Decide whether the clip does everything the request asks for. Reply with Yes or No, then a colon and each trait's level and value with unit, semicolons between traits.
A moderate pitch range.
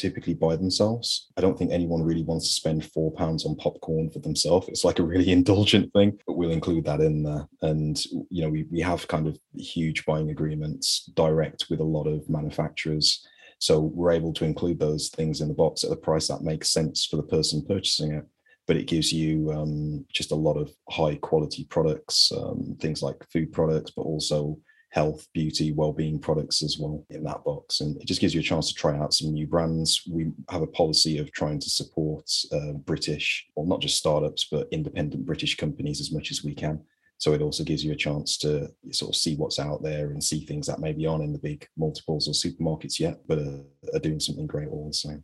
No: narrow, 1.3 semitones